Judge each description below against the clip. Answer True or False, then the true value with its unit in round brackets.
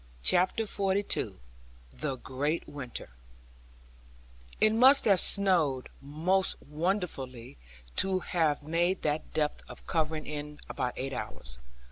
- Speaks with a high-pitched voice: False (155 Hz)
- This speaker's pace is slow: True (110 wpm)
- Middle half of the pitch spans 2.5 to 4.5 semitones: False (5.4 semitones)